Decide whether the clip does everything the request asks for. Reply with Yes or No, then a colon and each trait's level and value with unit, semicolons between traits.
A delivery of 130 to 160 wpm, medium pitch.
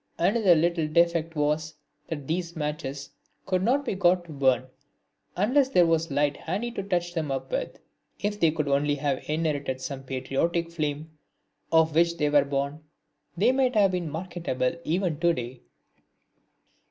No: average, 170 wpm; medium, 160 Hz